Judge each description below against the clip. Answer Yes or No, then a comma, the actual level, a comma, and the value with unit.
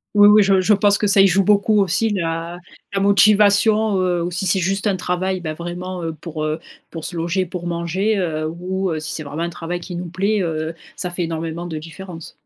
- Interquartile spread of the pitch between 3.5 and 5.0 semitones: No, average, 2.8 semitones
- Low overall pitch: No, medium, 180 Hz